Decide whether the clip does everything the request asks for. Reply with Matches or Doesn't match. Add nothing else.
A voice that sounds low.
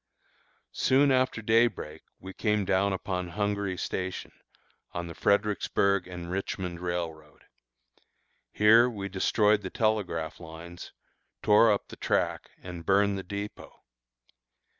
Matches